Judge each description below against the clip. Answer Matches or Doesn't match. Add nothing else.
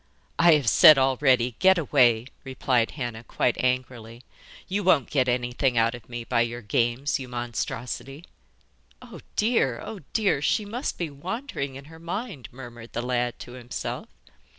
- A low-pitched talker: Matches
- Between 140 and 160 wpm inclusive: Matches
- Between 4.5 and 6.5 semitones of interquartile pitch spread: Doesn't match